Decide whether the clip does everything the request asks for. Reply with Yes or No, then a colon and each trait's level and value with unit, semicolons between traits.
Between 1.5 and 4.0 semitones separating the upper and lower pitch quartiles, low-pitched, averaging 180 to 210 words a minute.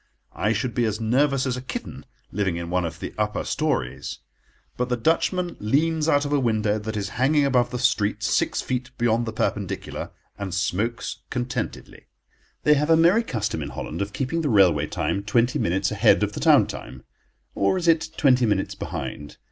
No: wide, 5.6 semitones; low, 120 Hz; average, 190 wpm